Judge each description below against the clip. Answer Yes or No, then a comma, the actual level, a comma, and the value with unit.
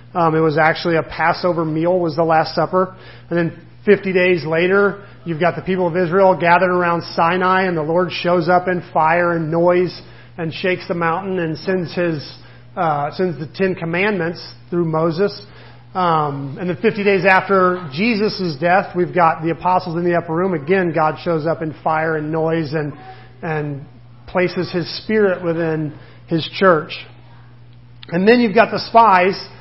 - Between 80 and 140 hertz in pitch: No, medium, 170 Hz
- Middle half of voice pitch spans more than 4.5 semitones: No, narrow, 2.5 semitones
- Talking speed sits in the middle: Yes, average, 175 wpm